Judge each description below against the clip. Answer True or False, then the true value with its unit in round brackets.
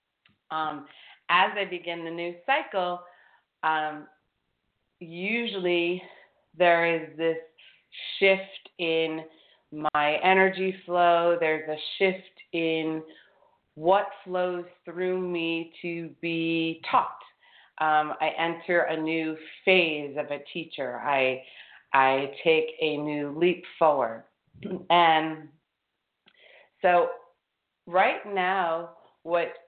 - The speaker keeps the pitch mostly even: True (2.3 semitones)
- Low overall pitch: False (165 Hz)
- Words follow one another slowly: True (100 wpm)